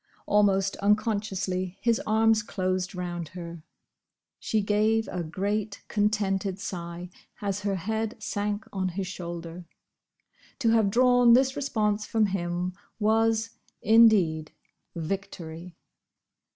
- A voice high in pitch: Yes, high, 200 Hz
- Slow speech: Yes, slow, 110 wpm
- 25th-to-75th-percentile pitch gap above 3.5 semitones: No, average, 3.2 semitones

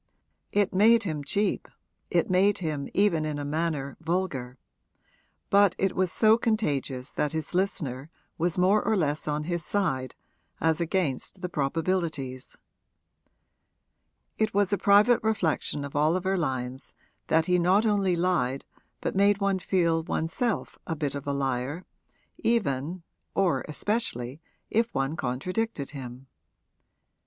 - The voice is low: No, medium, 170 Hz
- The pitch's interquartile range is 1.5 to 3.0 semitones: No, wide, 5.6 semitones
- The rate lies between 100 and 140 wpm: Yes, slow, 135 wpm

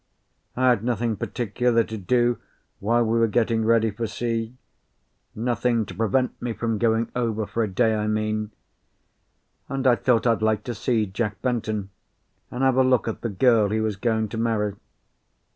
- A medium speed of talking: Yes, average, 175 wpm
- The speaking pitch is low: Yes, low, 115 Hz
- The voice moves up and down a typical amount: No, narrow, 2.0 semitones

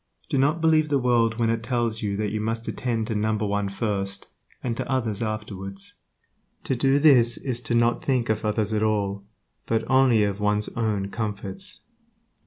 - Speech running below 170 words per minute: No, average, 190 wpm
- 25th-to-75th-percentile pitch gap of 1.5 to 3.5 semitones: Yes, average, 2.8 semitones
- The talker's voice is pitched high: No, low, 110 Hz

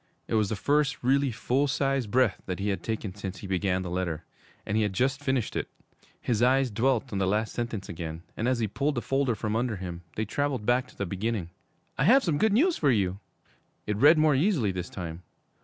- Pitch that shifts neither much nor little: No, wide, 5.7 semitones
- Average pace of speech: No, fast, 225 wpm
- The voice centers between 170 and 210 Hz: No, low, 115 Hz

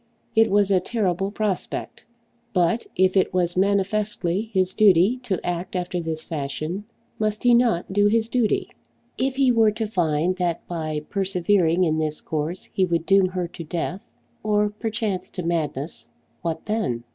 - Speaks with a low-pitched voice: No, medium, 185 Hz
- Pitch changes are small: No, average, 3.7 semitones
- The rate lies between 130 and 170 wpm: Yes, average, 160 wpm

